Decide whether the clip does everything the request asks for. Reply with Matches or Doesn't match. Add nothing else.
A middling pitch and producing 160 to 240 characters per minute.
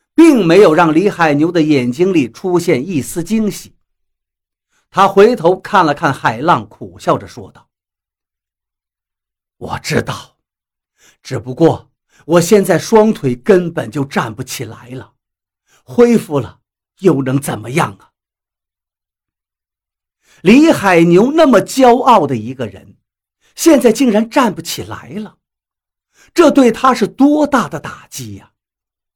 Matches